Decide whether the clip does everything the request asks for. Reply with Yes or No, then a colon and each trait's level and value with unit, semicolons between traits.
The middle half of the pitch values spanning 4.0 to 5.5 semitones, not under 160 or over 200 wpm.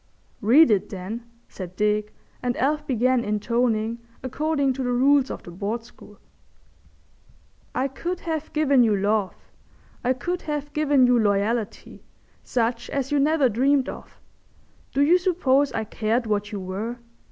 No: average, 4.8 semitones; average, 150 wpm